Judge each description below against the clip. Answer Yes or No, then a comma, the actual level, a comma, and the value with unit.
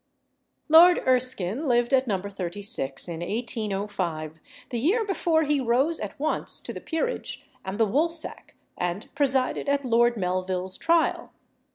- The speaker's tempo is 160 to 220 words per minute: No, average, 140 wpm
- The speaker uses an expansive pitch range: Yes, wide, 7.3 semitones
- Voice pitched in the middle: No, high, 240 Hz